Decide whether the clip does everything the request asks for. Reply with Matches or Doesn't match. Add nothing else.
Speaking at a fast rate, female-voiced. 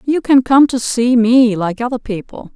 Matches